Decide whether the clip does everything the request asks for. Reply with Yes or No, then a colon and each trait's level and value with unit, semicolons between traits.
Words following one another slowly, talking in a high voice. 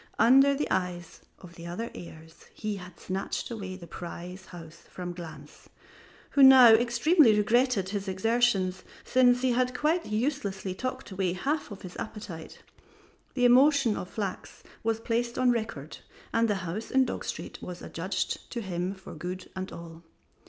No: average, 160 wpm; high, 205 Hz